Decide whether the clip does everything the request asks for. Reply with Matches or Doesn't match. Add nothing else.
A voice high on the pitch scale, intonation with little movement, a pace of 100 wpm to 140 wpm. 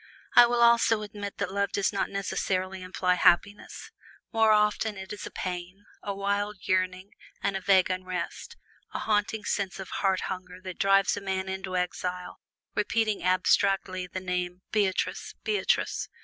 Doesn't match